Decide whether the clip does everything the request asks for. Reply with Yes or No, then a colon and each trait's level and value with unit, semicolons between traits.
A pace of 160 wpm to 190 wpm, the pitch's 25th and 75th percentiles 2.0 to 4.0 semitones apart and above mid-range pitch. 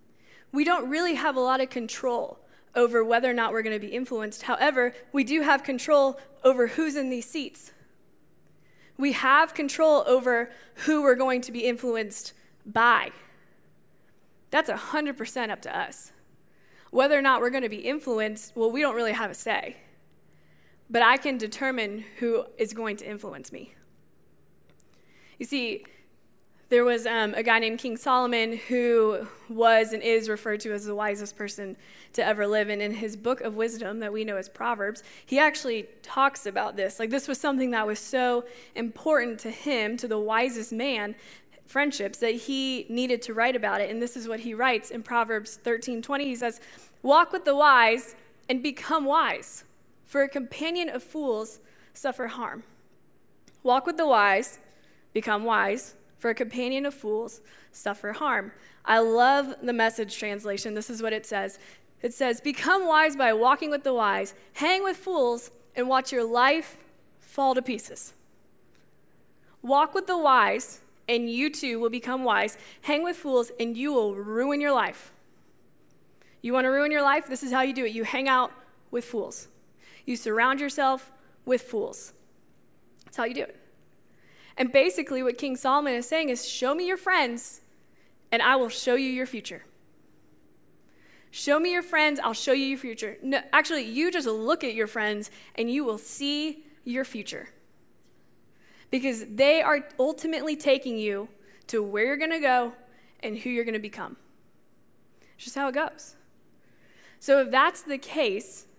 Yes: average, 170 wpm; average, 3.7 semitones; high, 245 Hz